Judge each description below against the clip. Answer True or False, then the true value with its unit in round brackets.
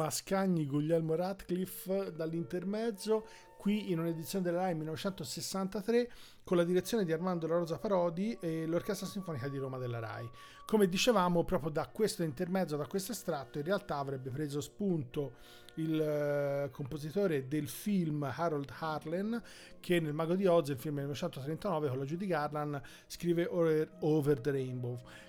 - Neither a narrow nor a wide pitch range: True (4.2 semitones)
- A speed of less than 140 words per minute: False (150 wpm)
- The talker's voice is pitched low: False (165 Hz)